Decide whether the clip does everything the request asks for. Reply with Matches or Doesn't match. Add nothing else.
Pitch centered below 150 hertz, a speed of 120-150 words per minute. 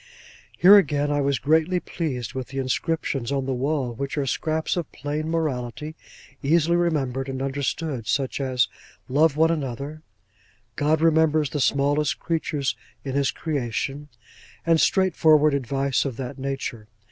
Matches